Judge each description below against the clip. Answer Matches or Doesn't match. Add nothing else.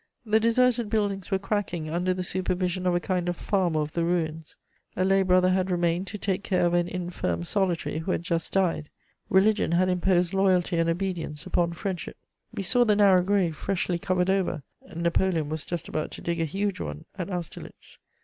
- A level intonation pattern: Matches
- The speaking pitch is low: Doesn't match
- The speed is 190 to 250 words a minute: Matches